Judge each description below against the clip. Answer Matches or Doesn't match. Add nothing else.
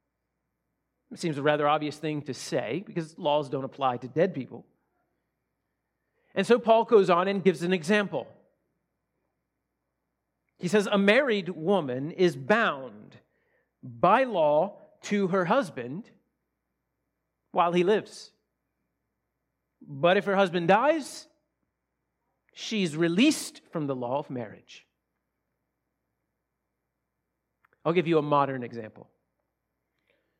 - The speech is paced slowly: Matches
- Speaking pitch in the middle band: Matches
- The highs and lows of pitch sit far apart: Matches